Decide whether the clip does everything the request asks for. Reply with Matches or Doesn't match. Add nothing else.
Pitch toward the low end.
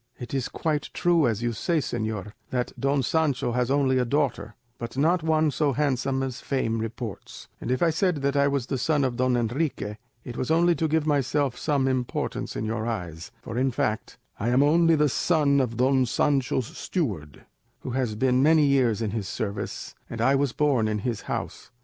Matches